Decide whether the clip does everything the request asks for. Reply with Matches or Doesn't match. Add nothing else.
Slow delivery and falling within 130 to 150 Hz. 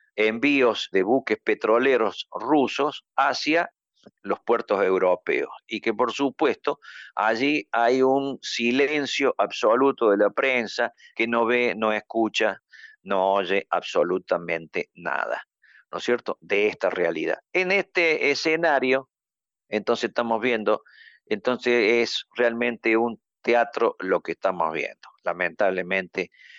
Doesn't match